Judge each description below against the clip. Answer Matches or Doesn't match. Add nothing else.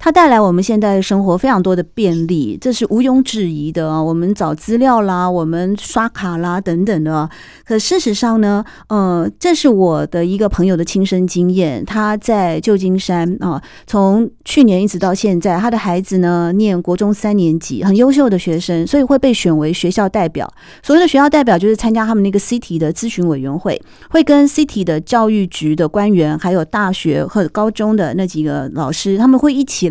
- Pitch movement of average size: Matches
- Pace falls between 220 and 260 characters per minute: Doesn't match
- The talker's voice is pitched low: Doesn't match